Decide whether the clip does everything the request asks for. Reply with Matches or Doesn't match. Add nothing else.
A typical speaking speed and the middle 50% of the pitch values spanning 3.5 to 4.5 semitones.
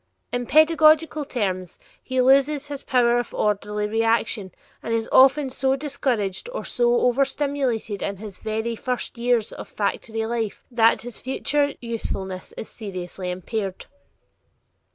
Doesn't match